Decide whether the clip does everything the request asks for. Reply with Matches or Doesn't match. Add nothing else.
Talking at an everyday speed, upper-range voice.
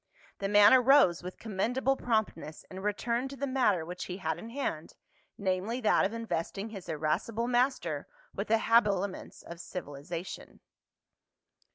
Matches